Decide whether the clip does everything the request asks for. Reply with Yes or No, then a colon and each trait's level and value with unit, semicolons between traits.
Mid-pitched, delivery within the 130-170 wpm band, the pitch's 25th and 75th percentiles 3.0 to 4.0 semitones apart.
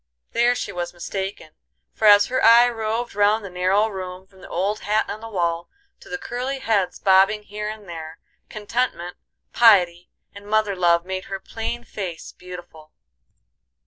No: high, 200 Hz; average, 165 wpm; average, 3.3 semitones